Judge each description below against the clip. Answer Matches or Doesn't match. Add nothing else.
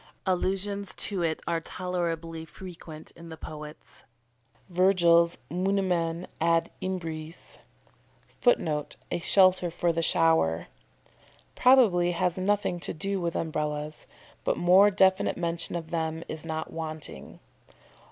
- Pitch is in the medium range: Matches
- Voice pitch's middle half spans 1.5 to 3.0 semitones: Matches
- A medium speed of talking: Doesn't match